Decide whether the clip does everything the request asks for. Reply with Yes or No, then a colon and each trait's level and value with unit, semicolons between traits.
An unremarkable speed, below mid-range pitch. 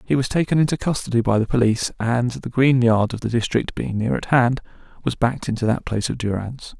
No: fast, 230 wpm; low, 120 Hz